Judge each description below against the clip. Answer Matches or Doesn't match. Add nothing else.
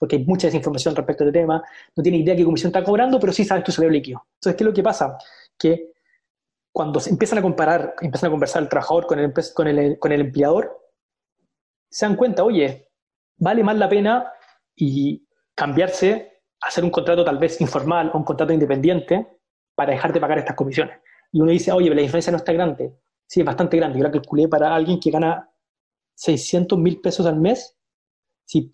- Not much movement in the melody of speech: Doesn't match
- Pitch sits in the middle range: Matches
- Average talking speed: Doesn't match